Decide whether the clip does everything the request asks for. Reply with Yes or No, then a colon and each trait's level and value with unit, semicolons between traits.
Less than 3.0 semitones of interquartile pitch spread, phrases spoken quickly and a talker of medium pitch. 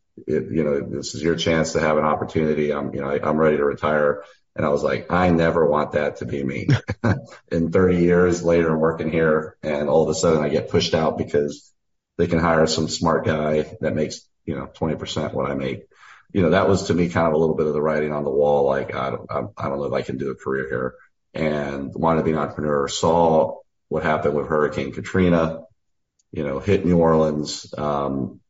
No: narrow, 2.4 semitones; fast, 230 wpm; very low, 80 Hz